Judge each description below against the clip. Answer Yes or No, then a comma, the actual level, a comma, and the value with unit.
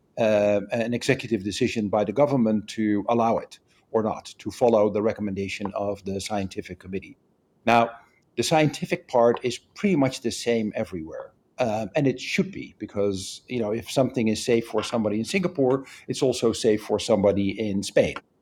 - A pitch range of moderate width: Yes, average, 3.3 semitones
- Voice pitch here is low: Yes, low, 115 Hz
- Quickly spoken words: No, average, 175 wpm